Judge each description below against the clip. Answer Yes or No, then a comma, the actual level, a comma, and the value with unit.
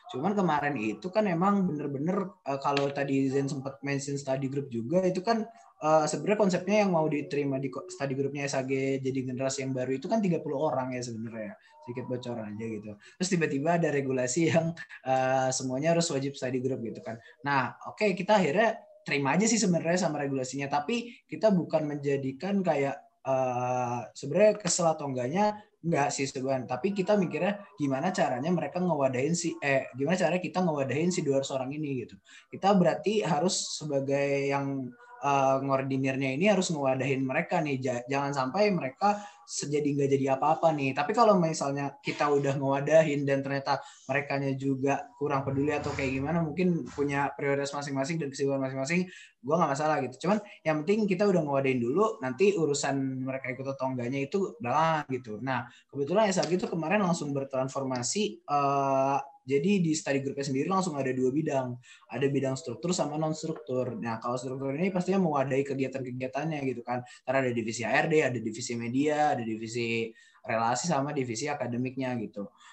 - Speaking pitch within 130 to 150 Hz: Yes, medium, 140 Hz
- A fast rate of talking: Yes, fast, 165 wpm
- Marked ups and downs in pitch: No, average, 4.0 semitones